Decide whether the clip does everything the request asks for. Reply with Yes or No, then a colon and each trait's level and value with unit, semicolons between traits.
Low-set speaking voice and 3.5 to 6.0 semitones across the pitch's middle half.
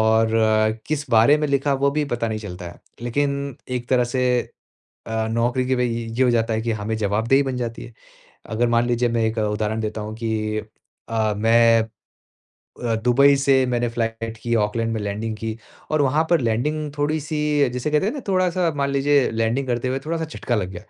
Yes: low, 120 Hz; average, 3.8 semitones